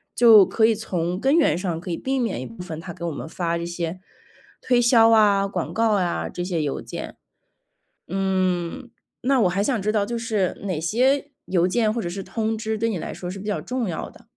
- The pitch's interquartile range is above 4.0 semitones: Yes, average, 4.5 semitones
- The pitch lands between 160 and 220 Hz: Yes, high, 200 Hz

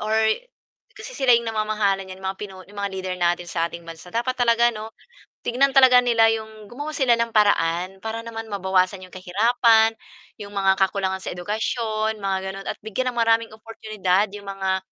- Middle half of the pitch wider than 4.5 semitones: No, average, 3.2 semitones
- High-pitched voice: Yes, high, 215 Hz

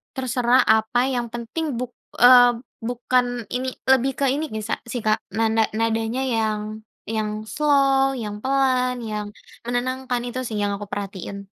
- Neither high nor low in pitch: No, high, 245 Hz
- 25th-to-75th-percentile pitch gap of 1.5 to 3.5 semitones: Yes, average, 2.8 semitones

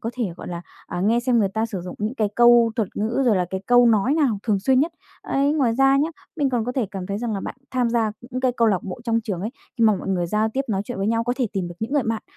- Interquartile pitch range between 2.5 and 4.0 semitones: Yes, average, 3.6 semitones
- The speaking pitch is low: No, high, 230 Hz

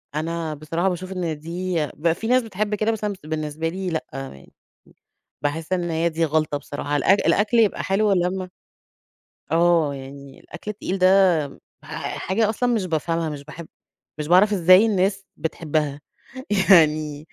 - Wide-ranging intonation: No, average, 3.8 semitones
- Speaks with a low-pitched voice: No, medium, 170 Hz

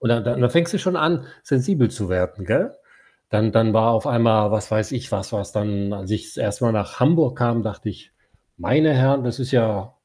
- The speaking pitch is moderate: No, low, 115 Hz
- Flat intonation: No, average, 3.4 semitones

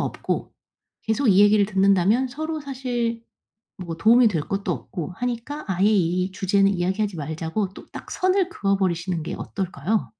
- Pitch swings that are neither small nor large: Yes, average, 4.5 semitones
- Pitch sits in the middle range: No, high, 200 Hz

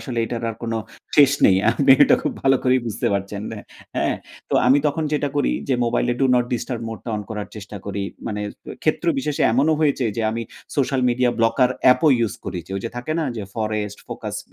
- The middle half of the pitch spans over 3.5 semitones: Yes, average, 4.0 semitones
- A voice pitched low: Yes, low, 120 Hz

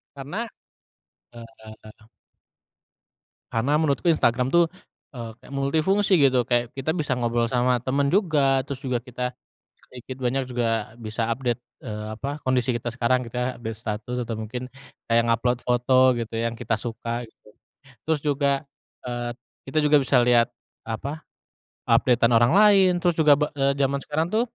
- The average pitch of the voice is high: No, low, 125 Hz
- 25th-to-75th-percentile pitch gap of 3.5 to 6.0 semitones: No, average, 3.1 semitones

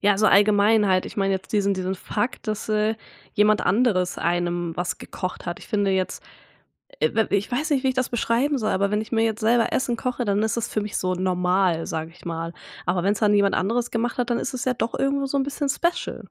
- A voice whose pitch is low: No, high, 210 Hz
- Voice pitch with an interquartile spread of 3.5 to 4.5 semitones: Yes, average, 4.2 semitones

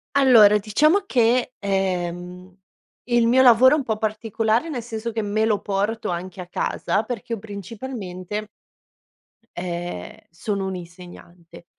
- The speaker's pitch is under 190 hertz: No, high, 210 Hz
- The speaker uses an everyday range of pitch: Yes, average, 4.3 semitones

